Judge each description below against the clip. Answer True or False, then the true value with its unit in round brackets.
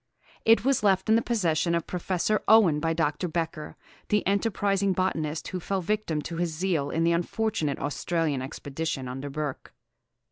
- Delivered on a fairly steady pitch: False (4.5 semitones)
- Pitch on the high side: False (170 Hz)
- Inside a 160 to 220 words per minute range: True (170 wpm)